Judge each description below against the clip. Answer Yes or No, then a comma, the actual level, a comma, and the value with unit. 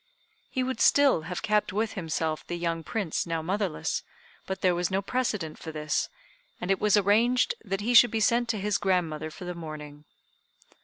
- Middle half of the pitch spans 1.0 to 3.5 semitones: No, average, 4.6 semitones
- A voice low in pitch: No, high, 190 Hz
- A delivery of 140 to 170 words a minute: No, average, 190 wpm